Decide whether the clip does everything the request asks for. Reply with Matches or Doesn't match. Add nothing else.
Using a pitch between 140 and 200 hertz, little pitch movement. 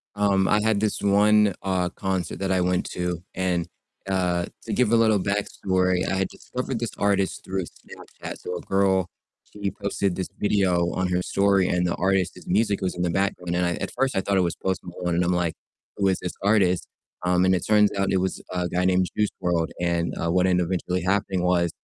Doesn't match